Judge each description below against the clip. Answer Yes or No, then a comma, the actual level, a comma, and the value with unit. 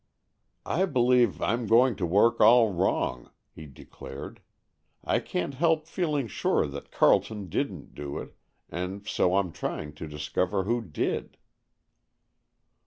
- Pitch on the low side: Yes, low, 100 Hz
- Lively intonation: Yes, wide, 6.9 semitones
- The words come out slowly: Yes, slow, 130 wpm